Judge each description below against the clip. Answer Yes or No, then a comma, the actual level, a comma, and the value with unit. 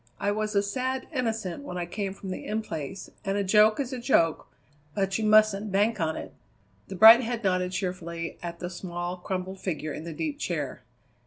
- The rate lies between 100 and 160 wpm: No, average, 200 wpm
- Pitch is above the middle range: Yes, high, 195 Hz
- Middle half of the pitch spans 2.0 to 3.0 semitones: No, average, 3.5 semitones